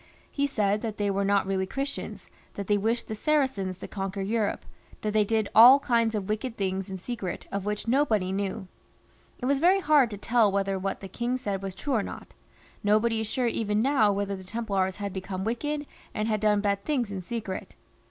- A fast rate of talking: Yes, fast, 210 wpm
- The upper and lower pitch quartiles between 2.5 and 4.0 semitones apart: Yes, average, 3.3 semitones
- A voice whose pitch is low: No, high, 210 Hz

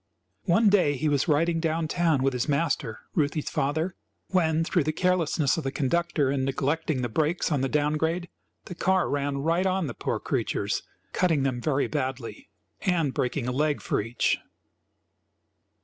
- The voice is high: No, medium, 150 Hz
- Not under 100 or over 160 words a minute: No, average, 170 wpm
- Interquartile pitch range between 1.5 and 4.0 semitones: Yes, average, 3.6 semitones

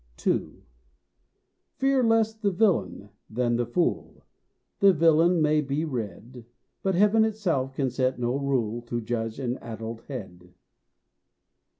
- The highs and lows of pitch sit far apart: Yes, wide, 7.2 semitones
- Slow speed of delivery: Yes, slow, 125 wpm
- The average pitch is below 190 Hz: Yes, low, 135 Hz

